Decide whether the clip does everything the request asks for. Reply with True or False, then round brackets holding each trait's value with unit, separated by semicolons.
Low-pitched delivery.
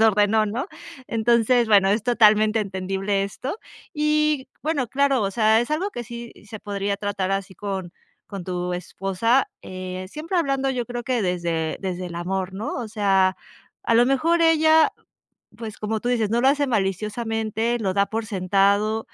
False (215 Hz)